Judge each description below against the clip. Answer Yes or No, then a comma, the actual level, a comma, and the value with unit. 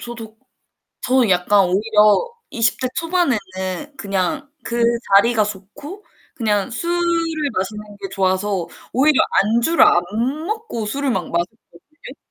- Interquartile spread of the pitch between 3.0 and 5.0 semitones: No, wide, 5.6 semitones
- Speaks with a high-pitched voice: Yes, high, 220 Hz